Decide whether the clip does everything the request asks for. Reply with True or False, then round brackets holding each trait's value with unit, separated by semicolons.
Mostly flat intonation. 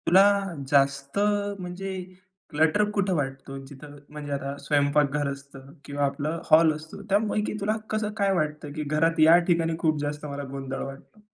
False (3.2 semitones)